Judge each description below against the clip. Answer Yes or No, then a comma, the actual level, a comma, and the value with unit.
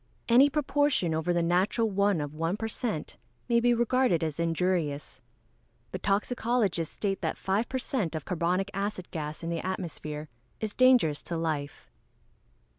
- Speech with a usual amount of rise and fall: No, wide, 5.8 semitones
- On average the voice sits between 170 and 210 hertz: Yes, medium, 185 Hz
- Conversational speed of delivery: Yes, average, 160 wpm